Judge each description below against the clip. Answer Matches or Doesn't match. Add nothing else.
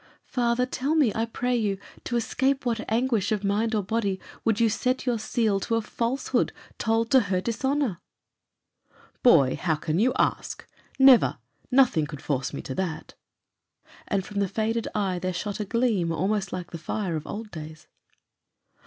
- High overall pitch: Matches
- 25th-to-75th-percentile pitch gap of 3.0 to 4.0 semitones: Doesn't match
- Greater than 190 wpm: Doesn't match